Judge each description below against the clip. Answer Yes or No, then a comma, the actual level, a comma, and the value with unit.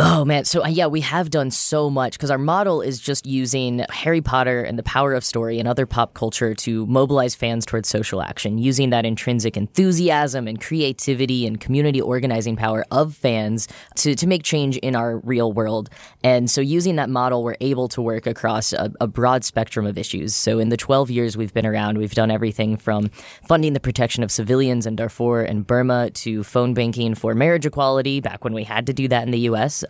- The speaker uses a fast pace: Yes, fast, 210 wpm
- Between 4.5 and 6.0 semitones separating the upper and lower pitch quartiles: No, average, 3.2 semitones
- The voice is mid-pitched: No, low, 120 Hz